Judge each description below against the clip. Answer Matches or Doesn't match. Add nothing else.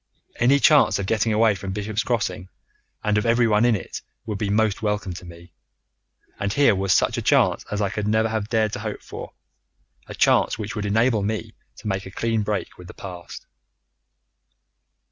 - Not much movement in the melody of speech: Matches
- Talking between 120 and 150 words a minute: Doesn't match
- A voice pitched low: Matches